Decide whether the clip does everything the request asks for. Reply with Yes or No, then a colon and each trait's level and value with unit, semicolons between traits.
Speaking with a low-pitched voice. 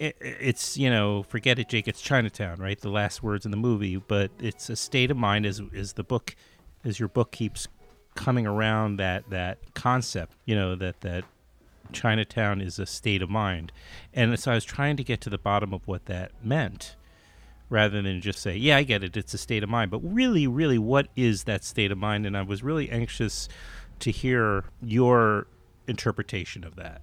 Yes: low, 105 Hz